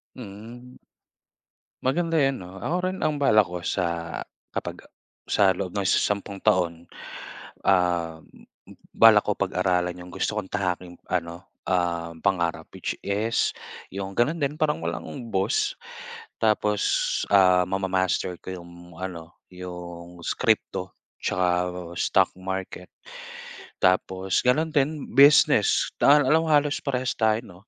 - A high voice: No, very low, 95 Hz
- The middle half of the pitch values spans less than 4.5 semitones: No, average, 5.0 semitones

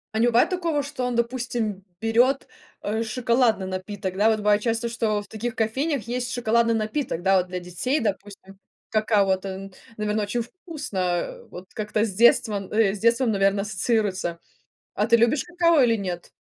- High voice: Yes, high, 220 Hz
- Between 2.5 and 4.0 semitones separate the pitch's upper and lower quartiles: Yes, average, 3.5 semitones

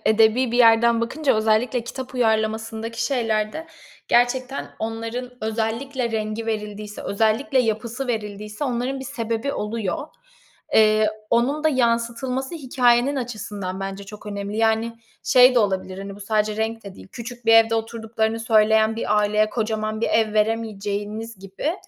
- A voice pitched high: Yes, high, 225 Hz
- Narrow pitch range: Yes, narrow, 2.2 semitones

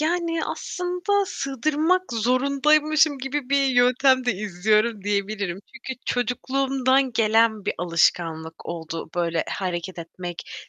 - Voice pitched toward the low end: No, high, 245 Hz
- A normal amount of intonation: No, wide, 6.6 semitones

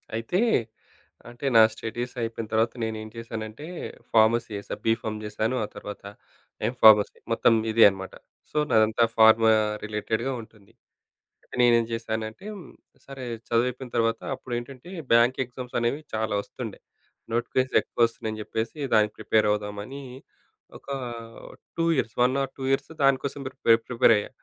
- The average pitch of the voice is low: Yes, low, 115 Hz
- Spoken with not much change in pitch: Yes, narrow, 2.3 semitones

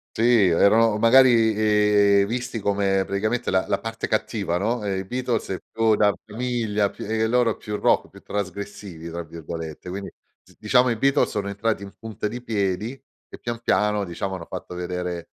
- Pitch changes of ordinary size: Yes, average, 3.1 semitones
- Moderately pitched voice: No, low, 105 Hz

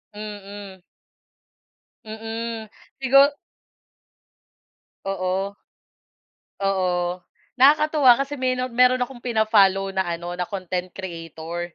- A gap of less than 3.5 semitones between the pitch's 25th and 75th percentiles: No, average, 5.2 semitones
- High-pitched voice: Yes, high, 200 Hz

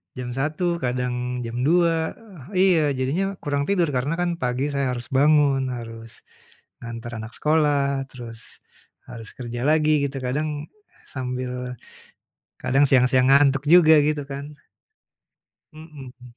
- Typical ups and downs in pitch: Yes, average, 3.5 semitones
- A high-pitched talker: No, low, 135 Hz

